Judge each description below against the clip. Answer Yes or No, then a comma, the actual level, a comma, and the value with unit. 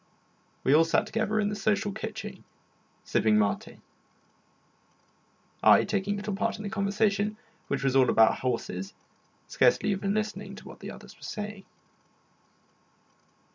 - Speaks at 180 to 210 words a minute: No, slow, 135 wpm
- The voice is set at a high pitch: Yes, high, 200 Hz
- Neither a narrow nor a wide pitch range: No, wide, 7.4 semitones